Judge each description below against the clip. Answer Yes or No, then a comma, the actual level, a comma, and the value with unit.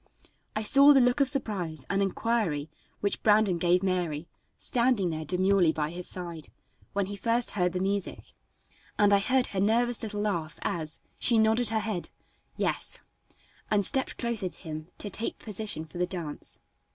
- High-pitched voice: Yes, high, 200 Hz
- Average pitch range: Yes, average, 4.3 semitones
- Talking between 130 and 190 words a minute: Yes, average, 170 wpm